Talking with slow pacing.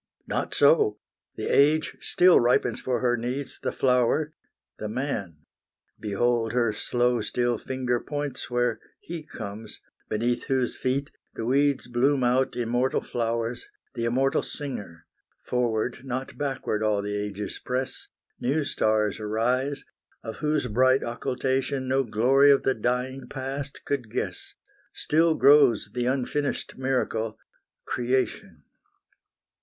Yes: slow, 125 wpm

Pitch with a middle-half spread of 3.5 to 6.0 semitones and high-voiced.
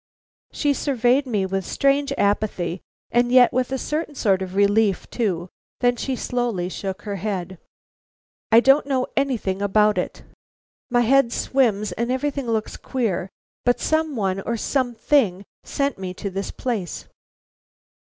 Yes: average, 5.1 semitones; high, 230 Hz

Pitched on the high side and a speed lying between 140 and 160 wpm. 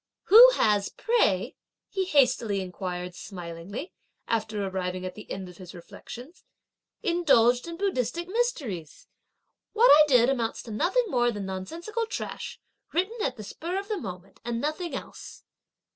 Yes: high, 240 Hz; average, 145 wpm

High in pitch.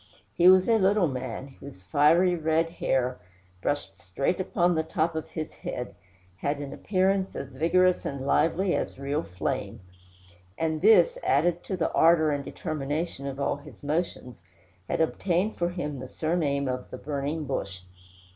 No: medium, 155 Hz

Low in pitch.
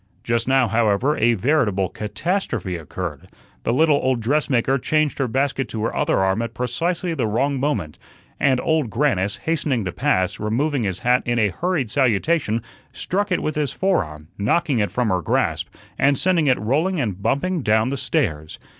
Yes: low, 125 Hz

